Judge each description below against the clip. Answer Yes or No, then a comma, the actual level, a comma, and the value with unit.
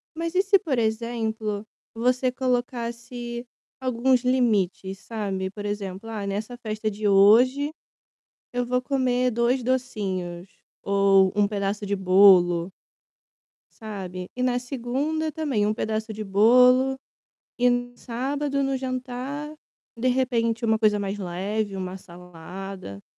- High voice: Yes, high, 230 Hz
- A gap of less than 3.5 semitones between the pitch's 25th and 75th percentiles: No, average, 4.2 semitones